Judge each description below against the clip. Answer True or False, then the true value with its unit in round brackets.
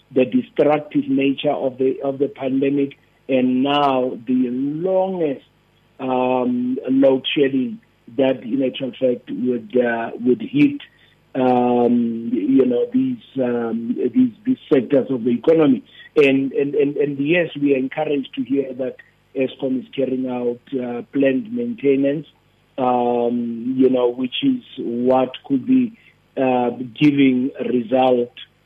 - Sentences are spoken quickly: False (135 wpm)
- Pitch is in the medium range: False (130 Hz)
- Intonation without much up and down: True (2.3 semitones)